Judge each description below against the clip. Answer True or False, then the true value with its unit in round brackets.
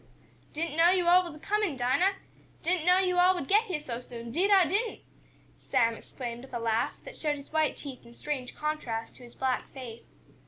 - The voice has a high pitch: True (300 Hz)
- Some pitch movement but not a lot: False (6.6 semitones)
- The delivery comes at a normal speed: False (210 wpm)